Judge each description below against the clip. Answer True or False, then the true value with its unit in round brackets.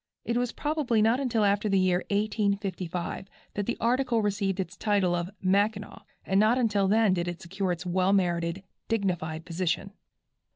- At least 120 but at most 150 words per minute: False (165 wpm)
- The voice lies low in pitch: False (200 Hz)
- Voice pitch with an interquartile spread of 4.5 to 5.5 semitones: False (3.1 semitones)